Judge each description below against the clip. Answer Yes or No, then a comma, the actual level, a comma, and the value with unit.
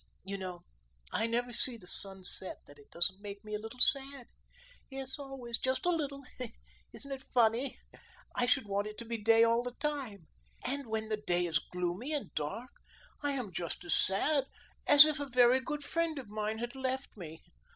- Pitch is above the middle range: Yes, high, 235 Hz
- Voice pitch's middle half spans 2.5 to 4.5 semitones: No, average, 5.2 semitones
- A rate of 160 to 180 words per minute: No, average, 195 wpm